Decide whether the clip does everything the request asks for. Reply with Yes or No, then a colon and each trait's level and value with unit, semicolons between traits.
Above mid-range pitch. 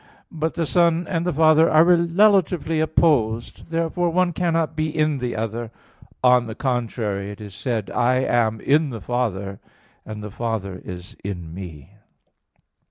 No: low, 125 Hz